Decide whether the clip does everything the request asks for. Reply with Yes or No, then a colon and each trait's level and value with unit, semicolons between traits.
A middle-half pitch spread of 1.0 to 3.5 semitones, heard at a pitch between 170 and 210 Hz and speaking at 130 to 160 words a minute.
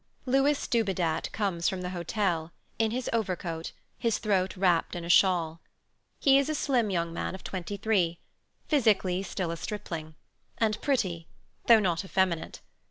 No: average, 4.5 semitones; high, 190 Hz; average, 150 wpm